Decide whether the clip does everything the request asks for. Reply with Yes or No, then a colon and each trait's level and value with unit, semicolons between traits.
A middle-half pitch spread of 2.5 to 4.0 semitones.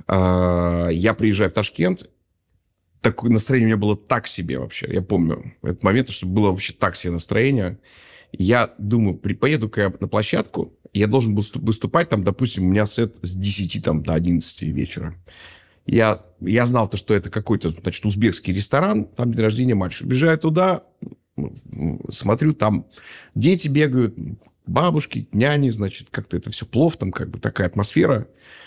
No: average, 4.7 semitones